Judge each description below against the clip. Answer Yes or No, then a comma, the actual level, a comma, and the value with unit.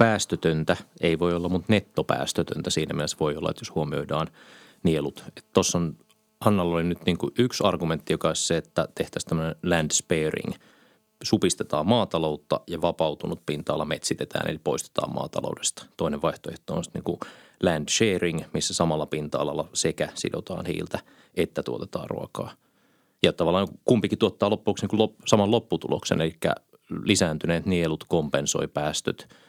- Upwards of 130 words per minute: Yes, average, 140 wpm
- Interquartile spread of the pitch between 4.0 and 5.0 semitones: Yes, average, 4.5 semitones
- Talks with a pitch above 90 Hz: No, very low, 85 Hz